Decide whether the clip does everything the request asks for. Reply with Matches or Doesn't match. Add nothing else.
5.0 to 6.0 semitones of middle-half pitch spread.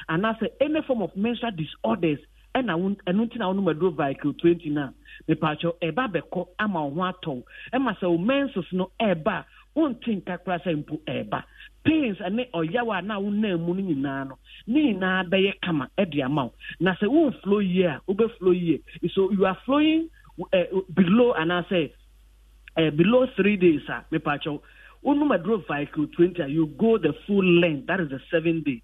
Matches